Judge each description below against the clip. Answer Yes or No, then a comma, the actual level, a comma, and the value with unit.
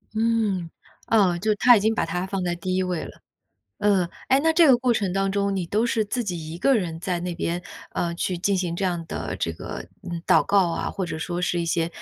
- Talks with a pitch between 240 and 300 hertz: No, medium, 185 Hz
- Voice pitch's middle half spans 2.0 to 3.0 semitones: No, average, 3.5 semitones